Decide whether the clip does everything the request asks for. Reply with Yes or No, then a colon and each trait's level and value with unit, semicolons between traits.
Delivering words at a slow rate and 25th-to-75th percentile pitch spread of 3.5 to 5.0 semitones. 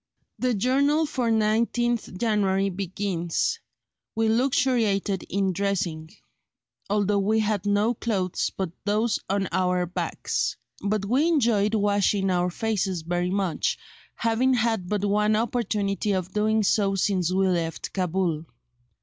No: slow, 125 wpm; average, 3.0 semitones